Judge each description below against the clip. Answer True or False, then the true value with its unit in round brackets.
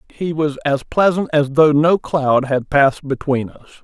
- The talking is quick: False (190 wpm)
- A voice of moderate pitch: True (145 Hz)